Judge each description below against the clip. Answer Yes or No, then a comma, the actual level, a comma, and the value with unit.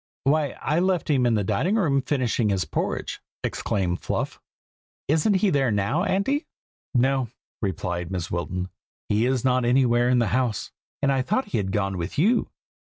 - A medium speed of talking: Yes, average, 170 wpm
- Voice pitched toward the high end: No, low, 125 Hz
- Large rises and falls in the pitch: Yes, wide, 6.9 semitones